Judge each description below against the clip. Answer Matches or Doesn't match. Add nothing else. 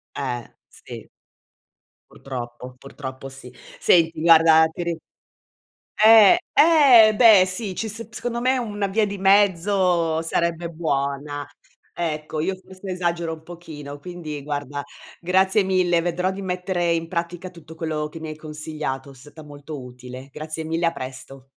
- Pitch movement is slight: Doesn't match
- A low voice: Doesn't match